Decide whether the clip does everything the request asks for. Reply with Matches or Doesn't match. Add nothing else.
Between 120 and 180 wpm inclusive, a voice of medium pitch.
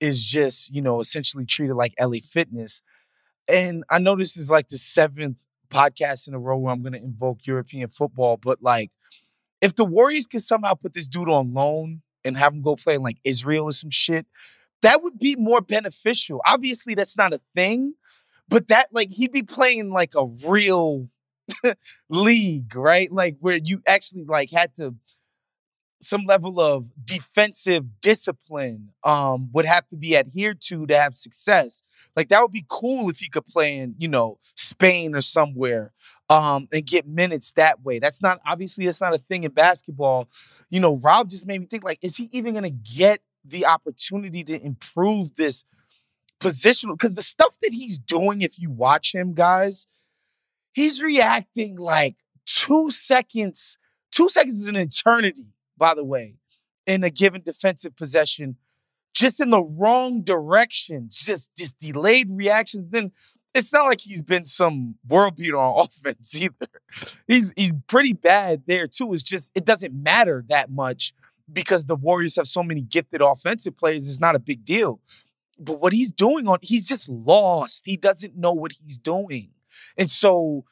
Matches